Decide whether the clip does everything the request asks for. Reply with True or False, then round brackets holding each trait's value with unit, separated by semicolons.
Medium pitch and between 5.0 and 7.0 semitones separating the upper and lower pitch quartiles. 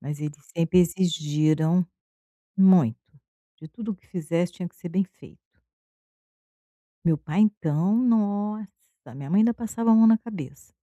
True (180 Hz; 5.3 semitones)